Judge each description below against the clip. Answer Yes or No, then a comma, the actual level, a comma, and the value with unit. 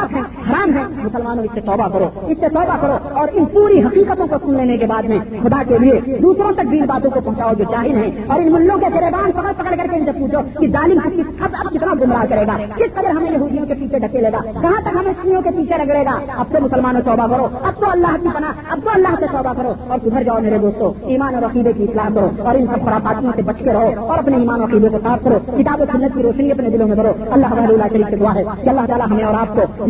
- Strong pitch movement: Yes, wide, 6.2 semitones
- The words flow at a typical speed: No, fast, 240 wpm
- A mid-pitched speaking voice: No, very high, 260 Hz